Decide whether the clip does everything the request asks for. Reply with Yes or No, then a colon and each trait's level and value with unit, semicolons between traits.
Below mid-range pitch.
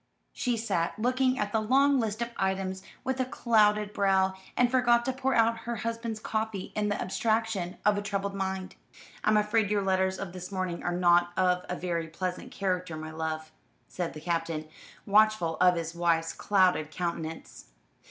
No: high, 195 Hz